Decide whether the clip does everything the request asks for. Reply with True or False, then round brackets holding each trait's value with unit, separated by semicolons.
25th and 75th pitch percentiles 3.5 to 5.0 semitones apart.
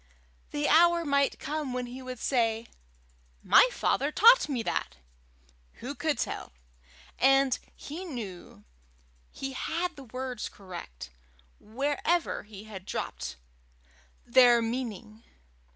True (4.6 semitones)